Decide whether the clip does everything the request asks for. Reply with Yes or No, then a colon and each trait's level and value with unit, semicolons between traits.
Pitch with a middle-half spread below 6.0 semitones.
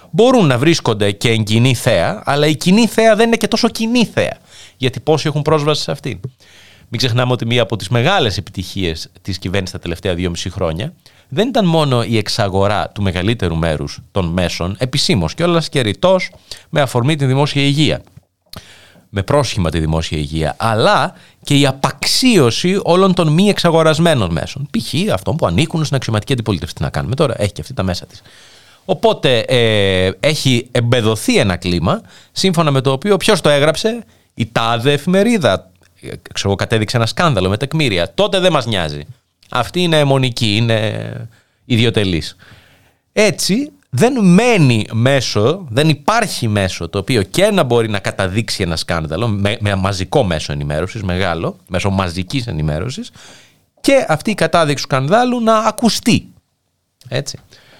No: wide, 8.5 semitones